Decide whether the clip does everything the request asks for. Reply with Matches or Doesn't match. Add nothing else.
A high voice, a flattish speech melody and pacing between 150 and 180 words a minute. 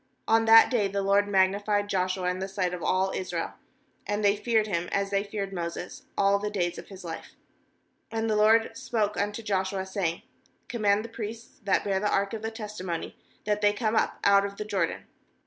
Doesn't match